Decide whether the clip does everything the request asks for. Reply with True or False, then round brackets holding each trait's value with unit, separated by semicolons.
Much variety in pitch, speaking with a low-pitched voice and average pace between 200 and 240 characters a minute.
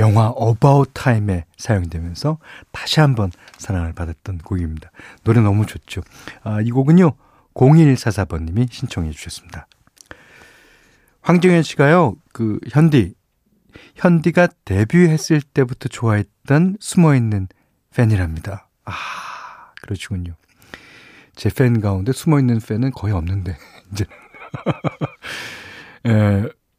True (6.3 semitones; 110 Hz; 235 characters per minute)